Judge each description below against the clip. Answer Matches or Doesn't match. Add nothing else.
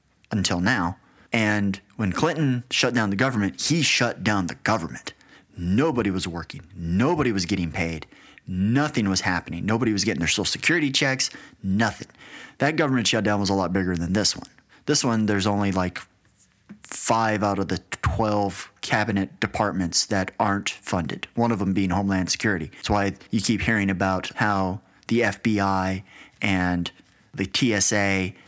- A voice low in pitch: Matches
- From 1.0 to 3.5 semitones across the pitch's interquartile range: Matches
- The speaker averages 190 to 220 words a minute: Doesn't match